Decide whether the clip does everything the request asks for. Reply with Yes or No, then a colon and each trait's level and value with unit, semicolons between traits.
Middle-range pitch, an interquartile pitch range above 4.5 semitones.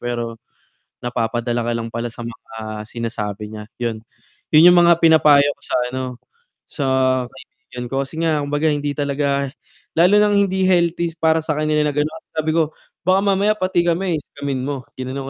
Yes: medium, 145 Hz; average, 5.3 semitones